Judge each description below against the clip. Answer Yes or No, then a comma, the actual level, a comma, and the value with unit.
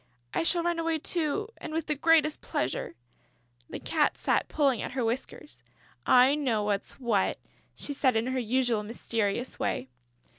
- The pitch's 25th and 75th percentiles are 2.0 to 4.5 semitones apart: No, average, 5.3 semitones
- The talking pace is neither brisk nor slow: Yes, average, 160 wpm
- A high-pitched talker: Yes, very high, 260 Hz